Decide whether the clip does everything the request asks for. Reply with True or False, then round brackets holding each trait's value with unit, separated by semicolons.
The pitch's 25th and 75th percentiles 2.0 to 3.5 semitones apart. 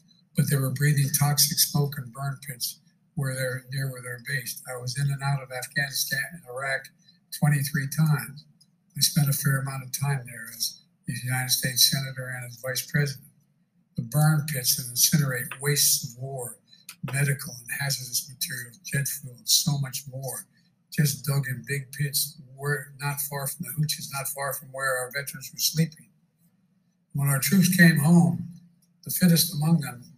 True (3.2 semitones)